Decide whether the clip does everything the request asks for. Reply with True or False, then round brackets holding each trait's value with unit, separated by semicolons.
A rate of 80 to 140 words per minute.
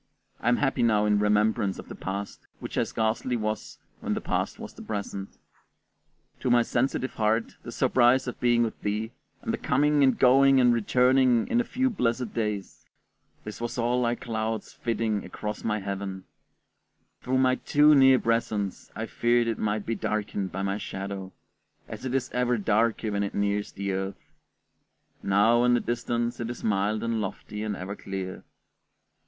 False (175 wpm)